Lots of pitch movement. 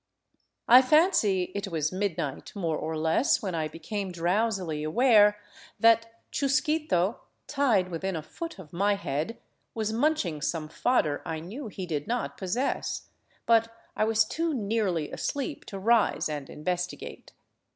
Yes: wide, 5.8 semitones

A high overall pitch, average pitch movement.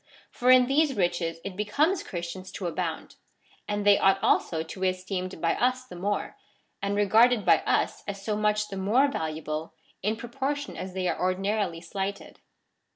Yes: high, 200 Hz; average, 3.8 semitones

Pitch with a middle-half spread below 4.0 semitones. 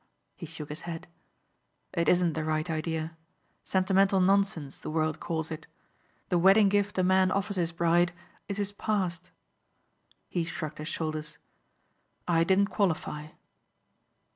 Yes: average, 3.3 semitones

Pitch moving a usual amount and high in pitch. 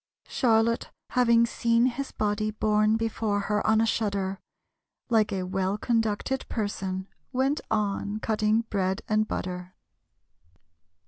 No: narrow, 2.2 semitones; high, 215 Hz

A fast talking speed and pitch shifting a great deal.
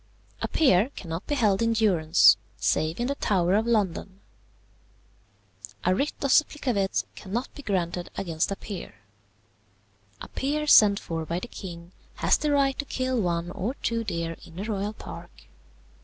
No: average, 160 wpm; wide, 5.9 semitones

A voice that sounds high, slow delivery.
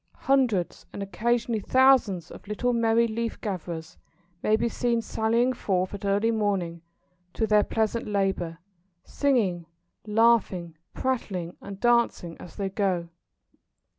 Yes: high, 210 Hz; slow, 125 wpm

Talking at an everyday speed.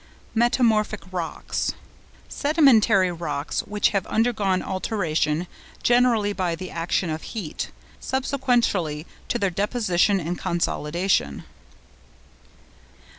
No: slow, 85 wpm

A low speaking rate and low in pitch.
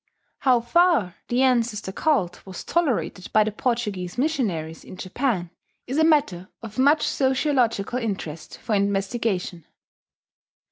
No: slow, 125 wpm; high, 225 Hz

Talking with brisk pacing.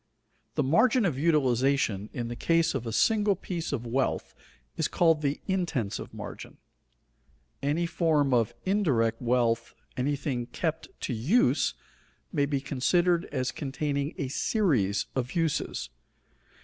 No: slow, 135 wpm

